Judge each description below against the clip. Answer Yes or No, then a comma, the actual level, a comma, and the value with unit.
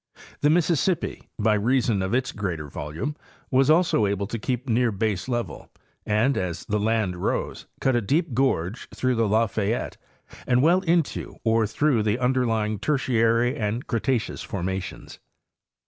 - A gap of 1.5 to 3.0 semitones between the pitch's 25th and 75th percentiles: No, average, 4.0 semitones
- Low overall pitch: Yes, low, 115 Hz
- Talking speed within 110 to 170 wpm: Yes, average, 145 wpm